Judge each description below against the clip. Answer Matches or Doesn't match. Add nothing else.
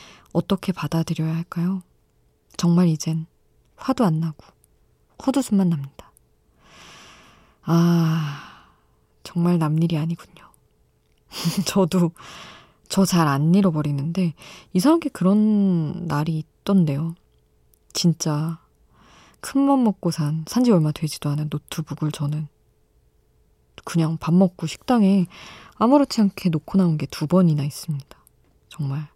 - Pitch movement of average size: Matches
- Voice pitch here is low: Doesn't match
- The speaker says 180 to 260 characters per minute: Matches